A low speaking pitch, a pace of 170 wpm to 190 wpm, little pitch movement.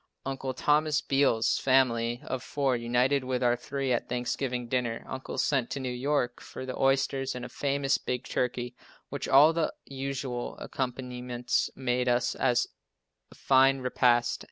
No: low, 130 Hz; average, 150 wpm; narrow, 1.7 semitones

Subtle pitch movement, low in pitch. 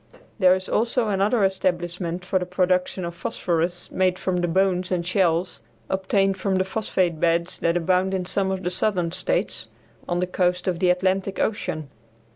No: narrow, 1.4 semitones; medium, 185 Hz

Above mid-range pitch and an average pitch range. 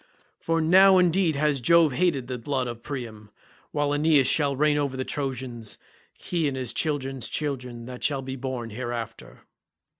No: low, 135 Hz; average, 3.5 semitones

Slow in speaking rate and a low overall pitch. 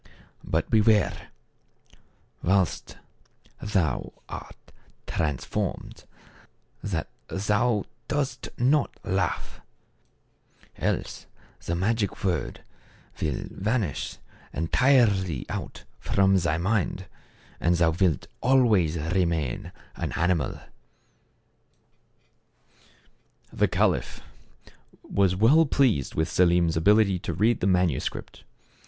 Yes: slow, 85 wpm; very low, 95 Hz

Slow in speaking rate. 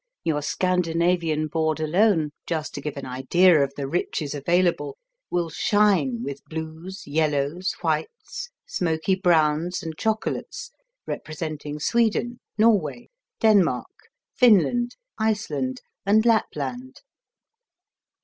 Yes: slow, 100 wpm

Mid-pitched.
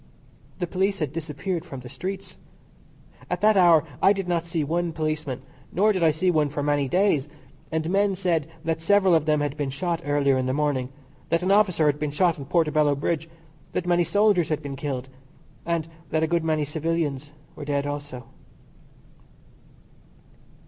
Yes: medium, 160 Hz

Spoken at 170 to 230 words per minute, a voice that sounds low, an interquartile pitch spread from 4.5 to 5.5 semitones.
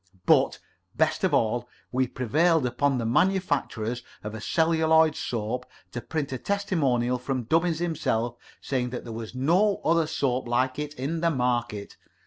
No: average, 150 wpm; low, 130 Hz; average, 5.0 semitones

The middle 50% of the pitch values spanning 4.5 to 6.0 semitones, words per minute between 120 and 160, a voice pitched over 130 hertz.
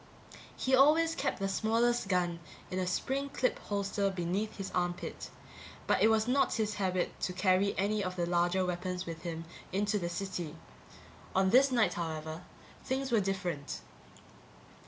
No: average, 3.7 semitones; average, 155 wpm; high, 190 Hz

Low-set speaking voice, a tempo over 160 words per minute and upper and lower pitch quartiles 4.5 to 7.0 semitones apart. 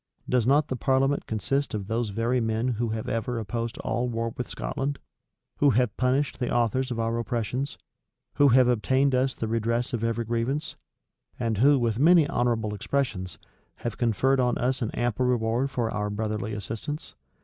No: low, 120 Hz; average, 175 wpm; narrow, 2.6 semitones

